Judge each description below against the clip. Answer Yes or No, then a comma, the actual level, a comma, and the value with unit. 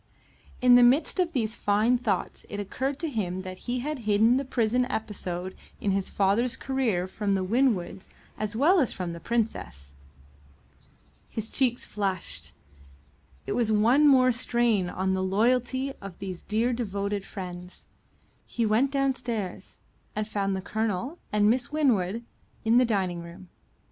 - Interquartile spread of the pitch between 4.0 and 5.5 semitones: Yes, average, 4.5 semitones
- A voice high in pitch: Yes, high, 220 Hz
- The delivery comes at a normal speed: Yes, average, 155 wpm